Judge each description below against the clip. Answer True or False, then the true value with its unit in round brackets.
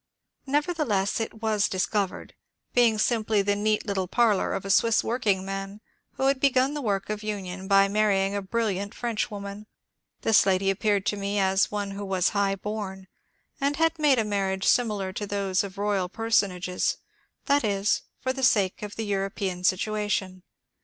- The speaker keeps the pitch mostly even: True (2.3 semitones)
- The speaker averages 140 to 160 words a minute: False (170 wpm)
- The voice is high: True (205 Hz)